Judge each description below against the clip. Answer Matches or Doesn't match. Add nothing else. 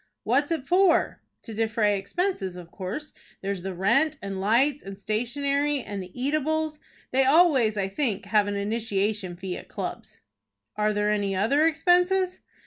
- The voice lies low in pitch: Doesn't match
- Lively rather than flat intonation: Matches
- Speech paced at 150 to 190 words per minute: Matches